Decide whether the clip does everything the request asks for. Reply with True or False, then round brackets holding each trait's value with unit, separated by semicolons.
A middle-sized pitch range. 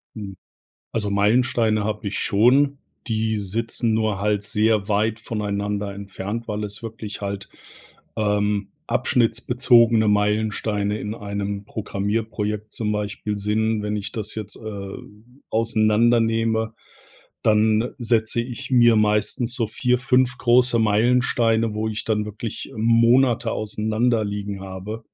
False (1.9 semitones)